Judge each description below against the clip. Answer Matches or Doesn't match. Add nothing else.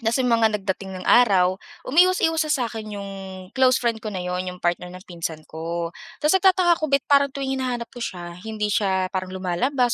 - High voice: Matches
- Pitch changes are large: Matches